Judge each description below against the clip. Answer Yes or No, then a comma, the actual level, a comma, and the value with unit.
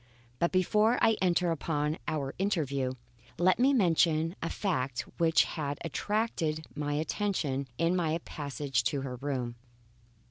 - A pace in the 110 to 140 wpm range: Yes, slow, 135 wpm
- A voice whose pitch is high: No, medium, 160 Hz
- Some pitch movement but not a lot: Yes, average, 4.4 semitones